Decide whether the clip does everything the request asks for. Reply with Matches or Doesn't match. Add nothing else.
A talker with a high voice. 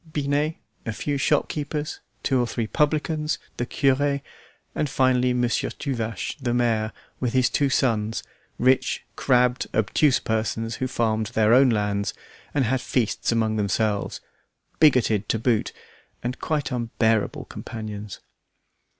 Doesn't match